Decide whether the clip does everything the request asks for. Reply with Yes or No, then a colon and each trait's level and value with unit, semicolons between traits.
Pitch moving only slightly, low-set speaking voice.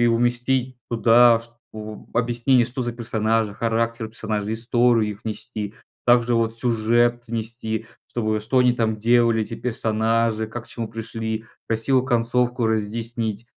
Yes: narrow, 1.4 semitones; low, 115 Hz